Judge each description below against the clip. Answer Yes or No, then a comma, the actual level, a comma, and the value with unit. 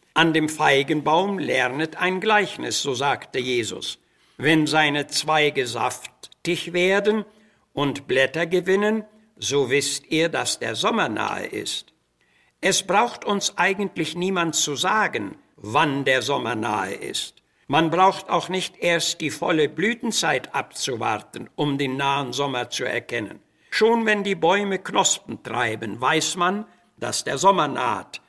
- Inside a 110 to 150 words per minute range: Yes, average, 135 wpm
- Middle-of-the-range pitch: Yes, medium, 160 Hz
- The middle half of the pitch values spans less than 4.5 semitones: No, average, 5.2 semitones